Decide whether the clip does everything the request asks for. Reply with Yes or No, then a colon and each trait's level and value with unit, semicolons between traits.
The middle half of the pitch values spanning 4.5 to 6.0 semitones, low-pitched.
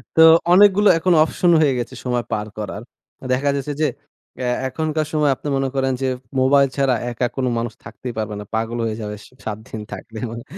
Yes: average, 4.8 semitones; low, 130 Hz